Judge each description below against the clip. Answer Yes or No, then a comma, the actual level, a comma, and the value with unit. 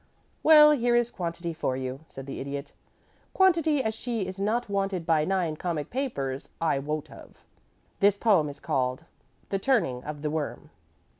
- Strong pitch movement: Yes, wide, 7.8 semitones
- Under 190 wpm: Yes, average, 165 wpm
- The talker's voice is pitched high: No, medium, 170 Hz